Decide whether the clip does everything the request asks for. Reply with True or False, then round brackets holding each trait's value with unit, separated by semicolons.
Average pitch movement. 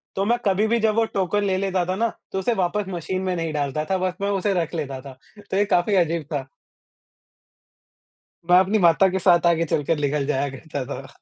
True (4.2 semitones)